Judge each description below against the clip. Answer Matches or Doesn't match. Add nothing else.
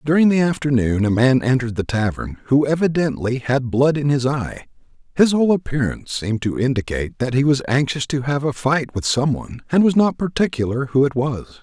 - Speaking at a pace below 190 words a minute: Doesn't match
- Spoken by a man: Matches